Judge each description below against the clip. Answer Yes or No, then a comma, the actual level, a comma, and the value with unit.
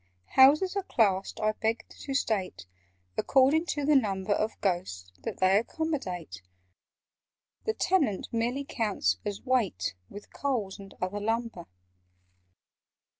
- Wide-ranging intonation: Yes, wide, 6.2 semitones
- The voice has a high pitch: Yes, high, 220 Hz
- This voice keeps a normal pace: No, slow, 125 wpm